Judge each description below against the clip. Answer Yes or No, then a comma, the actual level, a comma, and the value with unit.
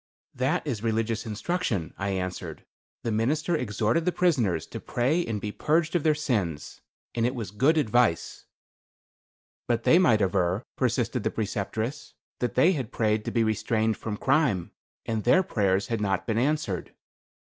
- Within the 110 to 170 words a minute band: Yes, average, 160 wpm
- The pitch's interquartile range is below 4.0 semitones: No, average, 5.3 semitones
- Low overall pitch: Yes, low, 115 Hz